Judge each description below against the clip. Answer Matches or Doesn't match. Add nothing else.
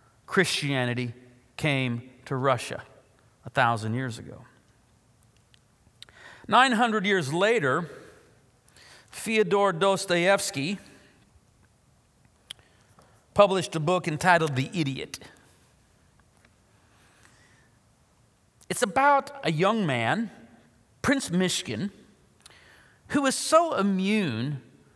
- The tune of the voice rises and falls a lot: Matches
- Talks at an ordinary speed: Doesn't match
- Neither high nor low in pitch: Matches